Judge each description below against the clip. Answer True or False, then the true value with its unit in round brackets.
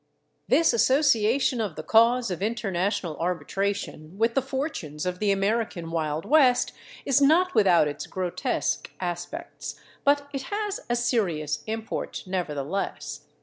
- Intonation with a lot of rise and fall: True (6.8 semitones)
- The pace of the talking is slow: True (130 wpm)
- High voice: True (210 Hz)